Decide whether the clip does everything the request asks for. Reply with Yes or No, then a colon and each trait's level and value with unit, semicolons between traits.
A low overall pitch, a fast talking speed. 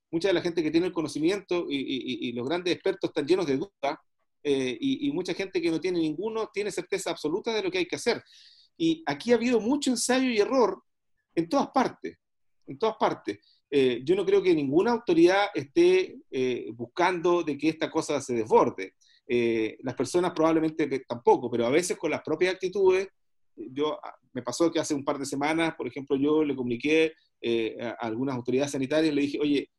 No: medium, 185 Hz; fast, 200 wpm